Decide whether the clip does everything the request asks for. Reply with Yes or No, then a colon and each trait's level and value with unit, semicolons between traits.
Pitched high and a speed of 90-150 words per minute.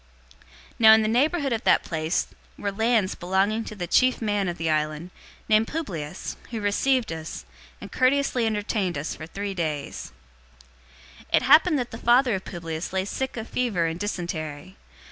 No: high, 205 Hz; average, 175 wpm